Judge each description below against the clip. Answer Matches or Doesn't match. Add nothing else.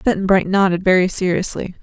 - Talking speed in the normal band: Matches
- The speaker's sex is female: Matches